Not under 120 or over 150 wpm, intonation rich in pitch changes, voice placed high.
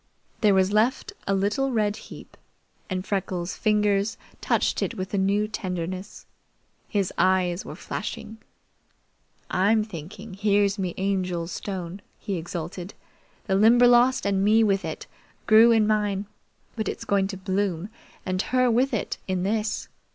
No: average, 145 wpm; narrow, 2.4 semitones; high, 200 Hz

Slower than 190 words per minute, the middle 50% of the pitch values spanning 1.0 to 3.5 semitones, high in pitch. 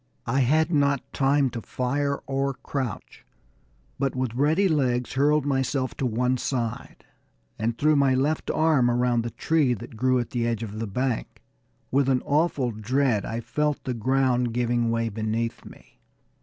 No: average, 165 wpm; average, 3.1 semitones; low, 130 Hz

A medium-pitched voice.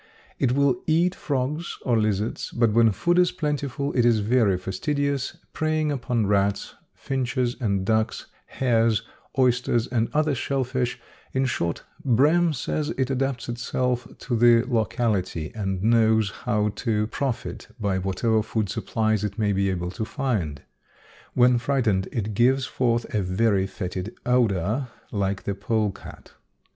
No: low, 115 Hz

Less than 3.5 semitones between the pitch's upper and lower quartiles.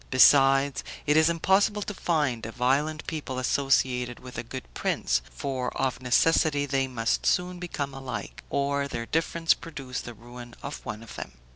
No: average, 3.8 semitones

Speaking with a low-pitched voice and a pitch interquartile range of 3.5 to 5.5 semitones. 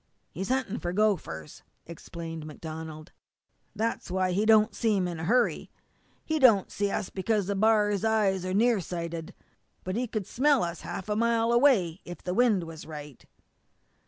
No: high, 195 Hz; average, 4.7 semitones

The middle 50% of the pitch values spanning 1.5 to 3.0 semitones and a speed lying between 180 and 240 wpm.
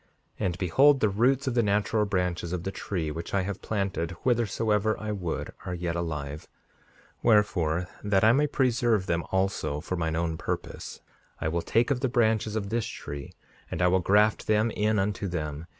No: average, 4.3 semitones; average, 185 wpm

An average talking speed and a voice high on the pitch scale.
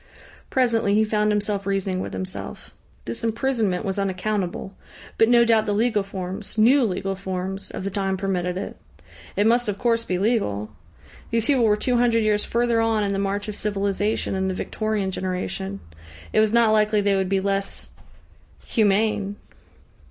Yes: average, 170 wpm; high, 205 Hz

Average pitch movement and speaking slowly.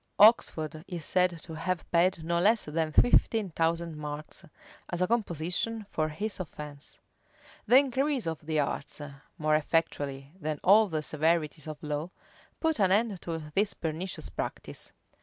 No: average, 4.0 semitones; average, 150 wpm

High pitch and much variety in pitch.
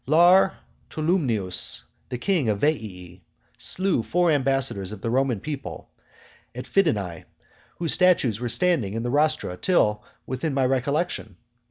No: low, 135 Hz; wide, 7.0 semitones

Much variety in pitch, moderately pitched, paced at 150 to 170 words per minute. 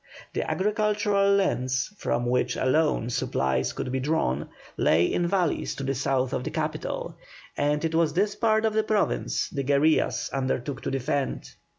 Yes: wide, 7.3 semitones; medium, 150 Hz; average, 165 wpm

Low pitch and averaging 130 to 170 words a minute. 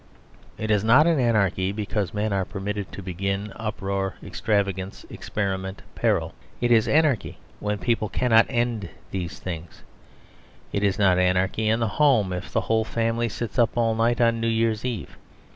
Yes: low, 105 Hz; average, 160 wpm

